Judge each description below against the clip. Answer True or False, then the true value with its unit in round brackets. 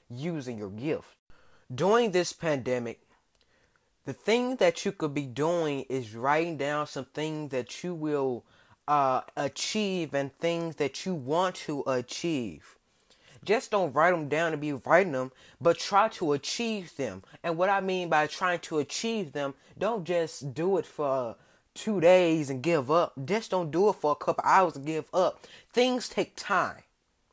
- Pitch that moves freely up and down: False (4.7 semitones)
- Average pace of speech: True (170 wpm)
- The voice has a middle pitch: True (155 Hz)